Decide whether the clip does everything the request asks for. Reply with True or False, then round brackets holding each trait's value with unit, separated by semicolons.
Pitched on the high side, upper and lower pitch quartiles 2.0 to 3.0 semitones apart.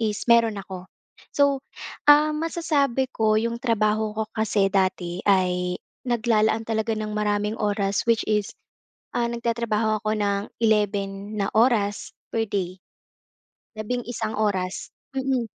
True (215 Hz; 2.5 semitones)